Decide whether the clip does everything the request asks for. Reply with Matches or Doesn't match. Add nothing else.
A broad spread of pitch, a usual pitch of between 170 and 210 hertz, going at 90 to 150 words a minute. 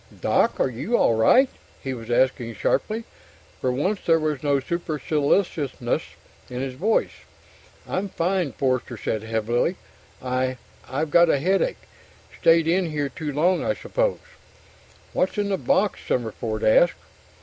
Doesn't match